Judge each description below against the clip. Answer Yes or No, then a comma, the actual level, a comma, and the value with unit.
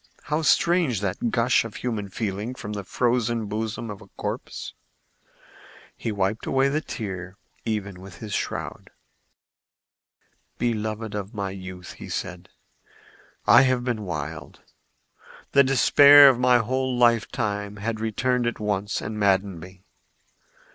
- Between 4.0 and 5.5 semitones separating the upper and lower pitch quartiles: No, average, 3.6 semitones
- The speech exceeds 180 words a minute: No, slow, 135 wpm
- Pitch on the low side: Yes, low, 110 Hz